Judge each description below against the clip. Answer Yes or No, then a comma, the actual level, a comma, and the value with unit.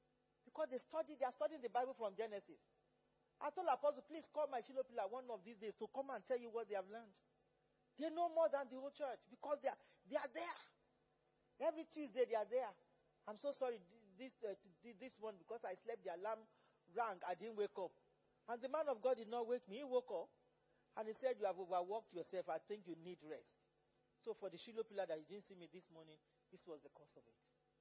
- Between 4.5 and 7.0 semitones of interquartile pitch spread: Yes, average, 4.8 semitones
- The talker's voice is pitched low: No, high, 230 Hz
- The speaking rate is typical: No, fast, 230 wpm